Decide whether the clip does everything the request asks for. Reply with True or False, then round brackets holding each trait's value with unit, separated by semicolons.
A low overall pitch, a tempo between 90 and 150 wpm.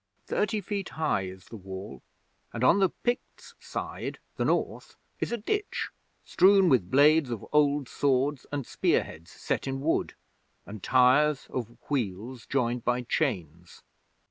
True (130 Hz; 145 wpm)